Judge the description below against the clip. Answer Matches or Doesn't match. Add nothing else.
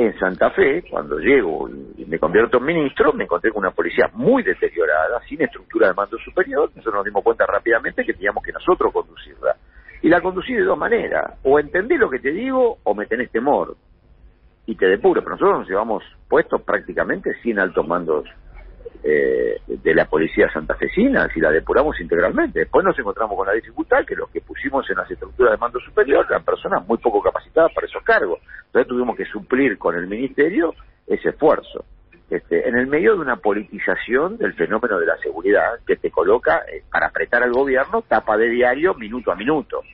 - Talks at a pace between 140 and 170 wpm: Doesn't match